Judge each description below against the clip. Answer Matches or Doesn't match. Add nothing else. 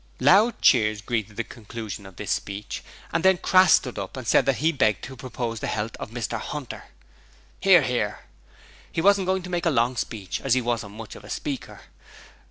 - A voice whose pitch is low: Matches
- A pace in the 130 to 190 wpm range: Doesn't match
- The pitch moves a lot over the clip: Matches